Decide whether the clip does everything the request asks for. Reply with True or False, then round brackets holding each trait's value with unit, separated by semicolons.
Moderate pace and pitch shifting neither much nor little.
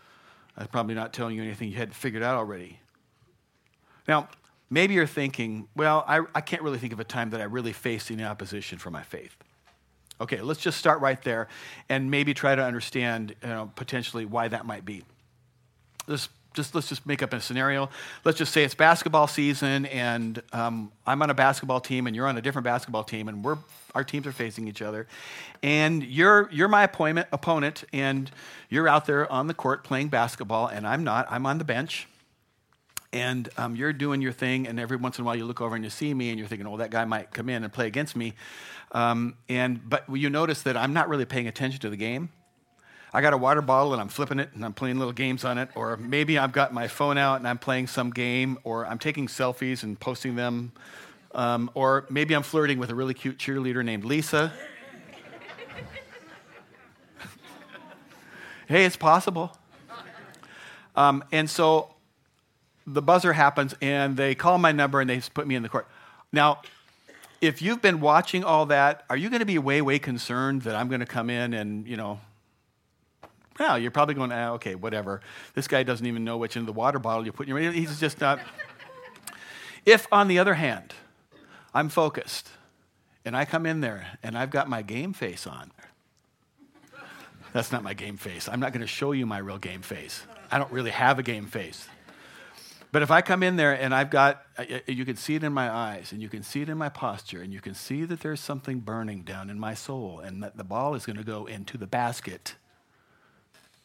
False (210 wpm; 3.9 semitones)